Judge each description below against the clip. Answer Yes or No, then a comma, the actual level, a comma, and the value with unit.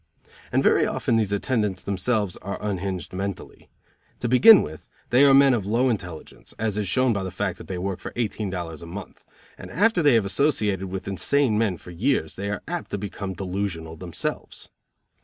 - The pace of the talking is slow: No, average, 195 wpm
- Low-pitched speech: Yes, low, 100 Hz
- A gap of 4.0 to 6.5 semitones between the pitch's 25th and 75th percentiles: Yes, average, 4.4 semitones